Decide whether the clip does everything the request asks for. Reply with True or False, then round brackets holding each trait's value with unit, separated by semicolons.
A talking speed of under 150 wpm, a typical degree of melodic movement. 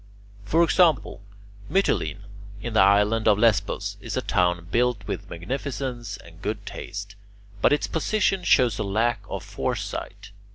True (140 wpm; 4.2 semitones)